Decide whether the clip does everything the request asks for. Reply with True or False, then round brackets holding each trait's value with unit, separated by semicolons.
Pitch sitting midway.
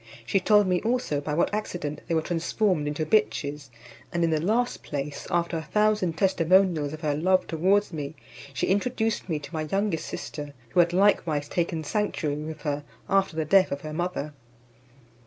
True (165 Hz)